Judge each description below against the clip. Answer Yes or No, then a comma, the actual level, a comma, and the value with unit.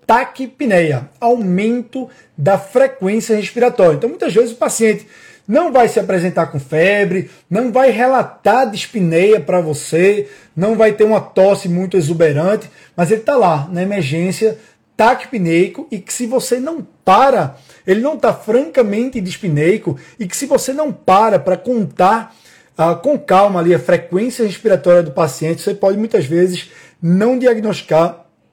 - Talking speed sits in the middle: Yes, average, 145 wpm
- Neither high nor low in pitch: No, high, 200 Hz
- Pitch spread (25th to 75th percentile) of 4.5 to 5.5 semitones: Yes, average, 5.1 semitones